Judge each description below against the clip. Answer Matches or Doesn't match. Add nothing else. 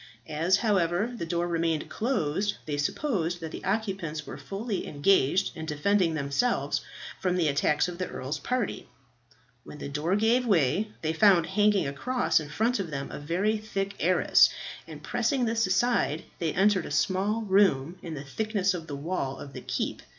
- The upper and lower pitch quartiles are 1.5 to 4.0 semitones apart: Doesn't match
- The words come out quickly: Doesn't match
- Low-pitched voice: Doesn't match